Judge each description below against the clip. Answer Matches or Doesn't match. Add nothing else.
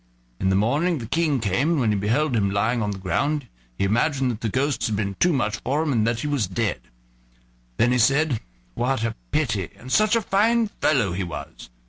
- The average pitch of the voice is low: Matches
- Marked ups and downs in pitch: Matches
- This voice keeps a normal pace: Doesn't match